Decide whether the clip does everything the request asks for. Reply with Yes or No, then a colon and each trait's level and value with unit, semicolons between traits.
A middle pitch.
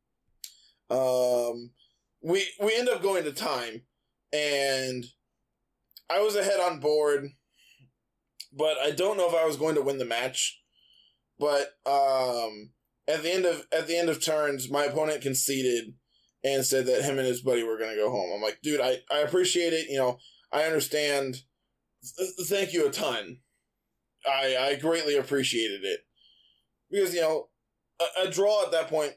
Yes: medium, 145 Hz